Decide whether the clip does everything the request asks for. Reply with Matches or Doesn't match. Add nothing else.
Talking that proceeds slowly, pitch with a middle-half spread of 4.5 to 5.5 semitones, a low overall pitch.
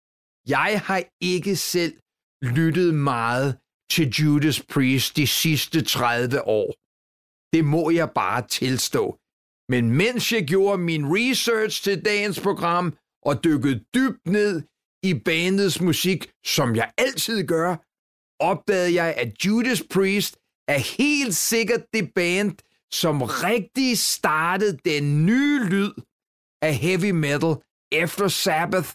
Doesn't match